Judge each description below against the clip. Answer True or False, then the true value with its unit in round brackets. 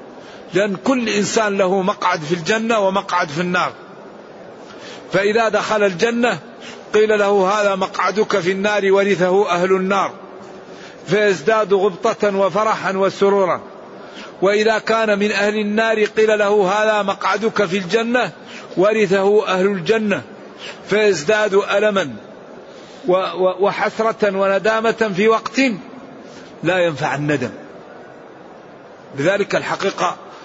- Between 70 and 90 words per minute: False (100 wpm)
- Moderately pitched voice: False (205 Hz)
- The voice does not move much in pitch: True (2.1 semitones)